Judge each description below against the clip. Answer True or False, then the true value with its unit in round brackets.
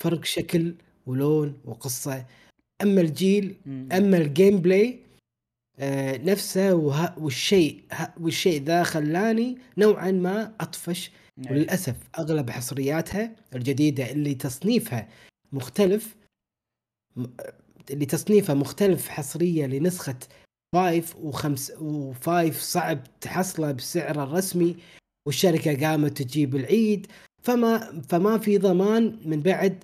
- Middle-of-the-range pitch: True (165 Hz)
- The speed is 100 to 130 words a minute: False (90 wpm)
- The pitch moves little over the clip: False (5.2 semitones)